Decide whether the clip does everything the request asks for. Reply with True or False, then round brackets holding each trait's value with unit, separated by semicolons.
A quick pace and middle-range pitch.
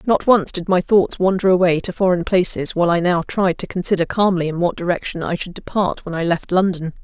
True (230 wpm; 180 Hz)